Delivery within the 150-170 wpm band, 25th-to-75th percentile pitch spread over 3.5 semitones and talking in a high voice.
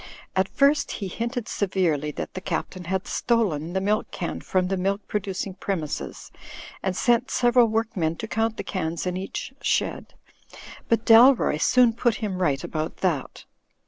Yes: average, 165 wpm; average, 4.1 semitones; high, 195 Hz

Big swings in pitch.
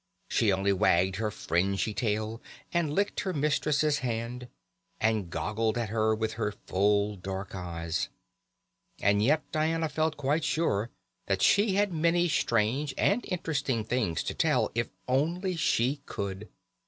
Yes: wide, 7.1 semitones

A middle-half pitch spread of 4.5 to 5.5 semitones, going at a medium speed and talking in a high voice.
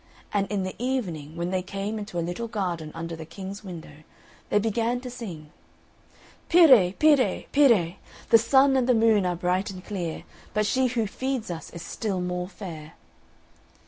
Yes: average, 4.9 semitones; average, 175 wpm; high, 195 Hz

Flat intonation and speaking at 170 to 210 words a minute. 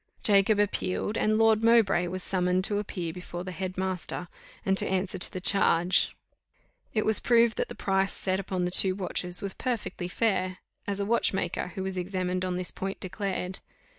Yes: narrow, 1.9 semitones; average, 185 wpm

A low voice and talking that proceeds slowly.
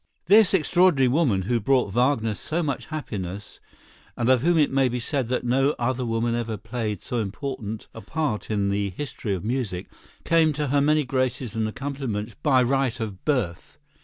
No: low, 125 Hz; average, 180 wpm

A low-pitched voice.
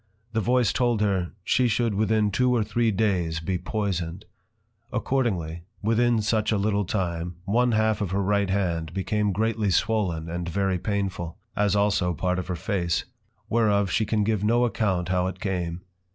Yes: low, 100 Hz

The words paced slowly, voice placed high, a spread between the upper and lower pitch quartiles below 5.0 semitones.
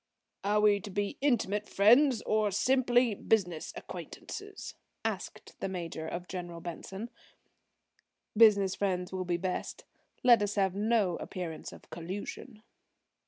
Yes: slow, 125 wpm; high, 200 Hz; average, 3.2 semitones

